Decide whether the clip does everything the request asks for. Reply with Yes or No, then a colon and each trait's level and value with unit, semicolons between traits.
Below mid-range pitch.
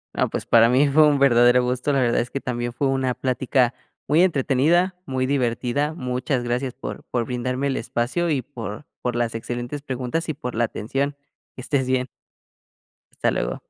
Yes: low, 130 Hz